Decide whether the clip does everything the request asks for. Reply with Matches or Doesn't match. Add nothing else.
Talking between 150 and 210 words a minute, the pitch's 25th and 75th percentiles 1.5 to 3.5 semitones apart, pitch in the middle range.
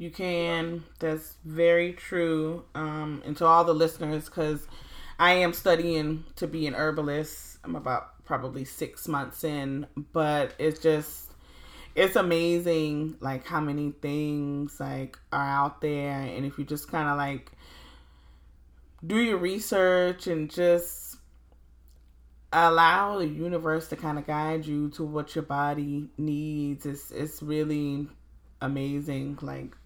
Doesn't match